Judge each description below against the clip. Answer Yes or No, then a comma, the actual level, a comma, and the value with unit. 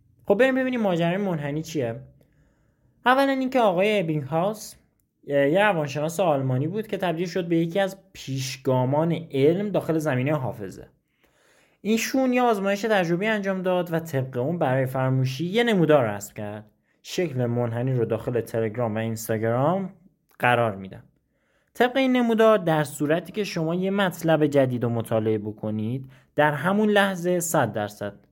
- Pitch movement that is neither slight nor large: No, wide, 7.5 semitones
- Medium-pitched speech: Yes, medium, 155 Hz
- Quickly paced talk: No, average, 145 wpm